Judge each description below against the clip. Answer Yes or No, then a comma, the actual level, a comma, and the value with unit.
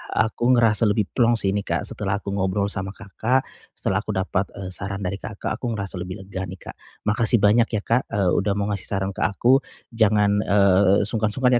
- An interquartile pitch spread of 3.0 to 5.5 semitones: No, narrow, 2.4 semitones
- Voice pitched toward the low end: Yes, low, 100 Hz